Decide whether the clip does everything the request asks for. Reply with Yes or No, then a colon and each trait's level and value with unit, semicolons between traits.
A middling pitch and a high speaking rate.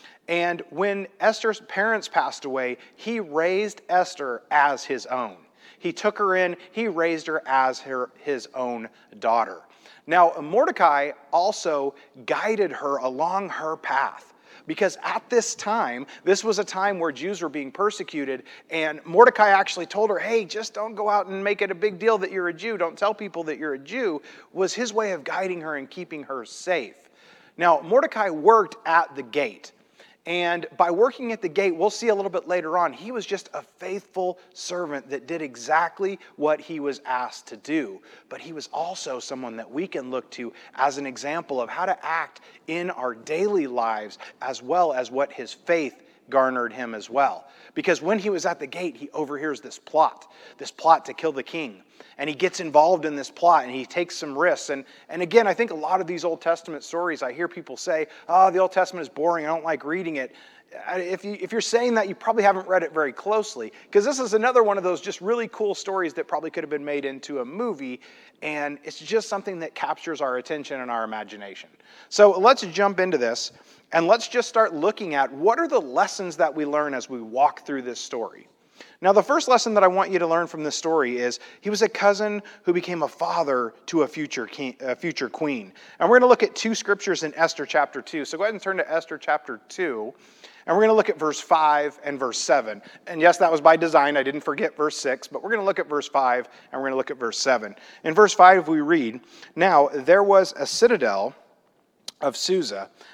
Yes: medium, 175 Hz; fast, 215 wpm